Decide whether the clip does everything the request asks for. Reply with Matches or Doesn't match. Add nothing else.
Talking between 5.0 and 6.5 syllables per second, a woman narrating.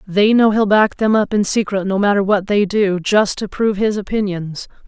Matches